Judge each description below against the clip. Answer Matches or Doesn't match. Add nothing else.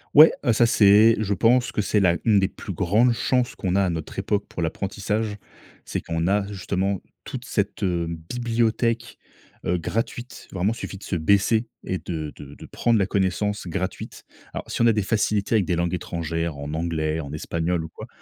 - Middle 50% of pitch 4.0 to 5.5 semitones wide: Matches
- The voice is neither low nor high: Doesn't match